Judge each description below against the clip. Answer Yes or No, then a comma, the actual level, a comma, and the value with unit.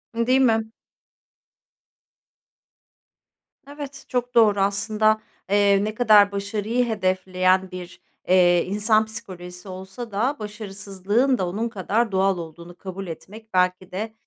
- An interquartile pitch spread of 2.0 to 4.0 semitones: Yes, average, 3.0 semitones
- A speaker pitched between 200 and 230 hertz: Yes, high, 205 Hz